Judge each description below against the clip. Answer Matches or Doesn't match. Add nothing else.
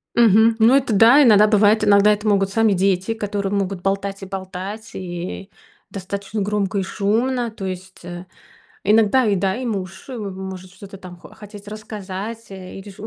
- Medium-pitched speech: Doesn't match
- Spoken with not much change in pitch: Matches